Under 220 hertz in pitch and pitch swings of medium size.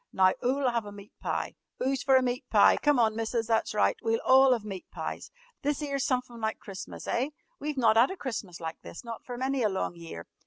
No: high, 235 Hz; average, 3.8 semitones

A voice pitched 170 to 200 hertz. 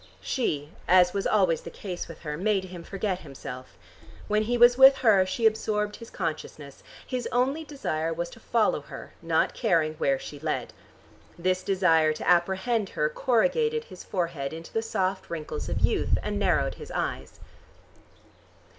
Yes: high, 190 Hz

